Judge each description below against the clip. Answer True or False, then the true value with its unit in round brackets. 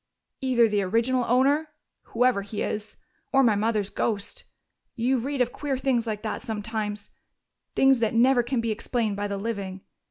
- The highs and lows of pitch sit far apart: False (3.4 semitones)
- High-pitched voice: True (230 Hz)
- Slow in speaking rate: False (165 wpm)